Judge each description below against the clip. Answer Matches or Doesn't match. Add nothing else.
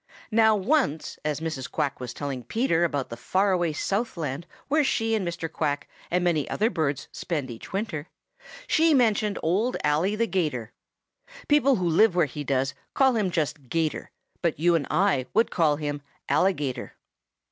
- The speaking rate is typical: Matches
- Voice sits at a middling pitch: Matches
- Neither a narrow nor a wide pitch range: Doesn't match